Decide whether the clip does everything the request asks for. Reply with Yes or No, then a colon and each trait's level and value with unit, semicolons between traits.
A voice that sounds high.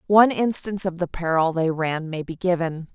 No: medium, 175 Hz